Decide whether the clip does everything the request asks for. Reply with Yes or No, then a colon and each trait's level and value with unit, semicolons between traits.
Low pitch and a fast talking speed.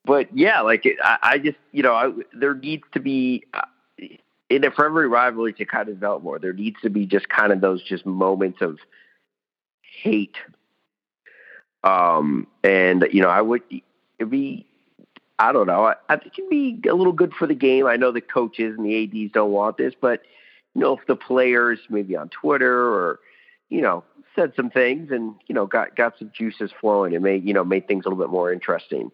Yes: low, 120 Hz; fast, 210 wpm